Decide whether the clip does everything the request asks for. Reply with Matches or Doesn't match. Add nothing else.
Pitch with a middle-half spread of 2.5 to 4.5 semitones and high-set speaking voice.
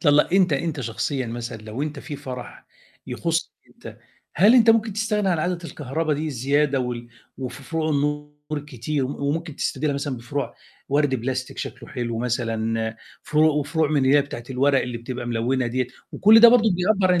Doesn't match